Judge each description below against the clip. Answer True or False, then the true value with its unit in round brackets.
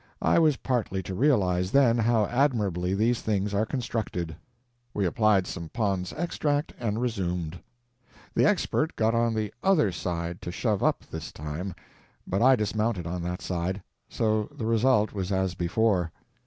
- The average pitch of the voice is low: True (105 Hz)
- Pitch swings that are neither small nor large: True (4.4 semitones)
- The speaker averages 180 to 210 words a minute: False (155 wpm)